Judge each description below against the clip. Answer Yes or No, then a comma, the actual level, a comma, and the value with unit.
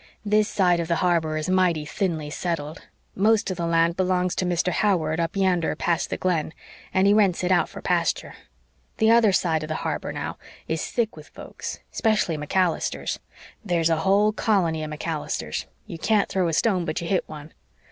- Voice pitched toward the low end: No, medium, 175 Hz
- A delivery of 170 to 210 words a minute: Yes, average, 190 wpm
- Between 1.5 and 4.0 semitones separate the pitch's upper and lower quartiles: Yes, average, 3.1 semitones